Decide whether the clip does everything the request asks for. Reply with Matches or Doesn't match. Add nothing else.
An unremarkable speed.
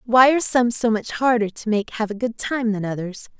Doesn't match